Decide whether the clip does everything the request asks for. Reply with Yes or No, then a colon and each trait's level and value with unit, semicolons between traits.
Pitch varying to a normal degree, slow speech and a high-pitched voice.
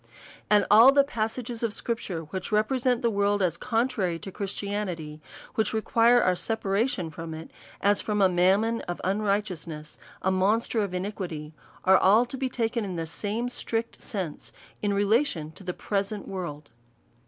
No: average, 3.8 semitones; average, 165 wpm; high, 205 Hz